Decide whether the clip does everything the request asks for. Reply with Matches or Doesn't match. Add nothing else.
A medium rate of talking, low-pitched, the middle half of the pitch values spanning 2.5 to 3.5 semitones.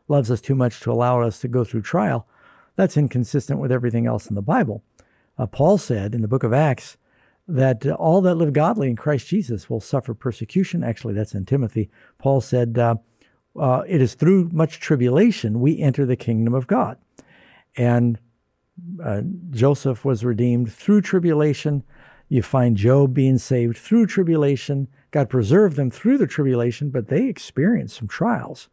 Doesn't match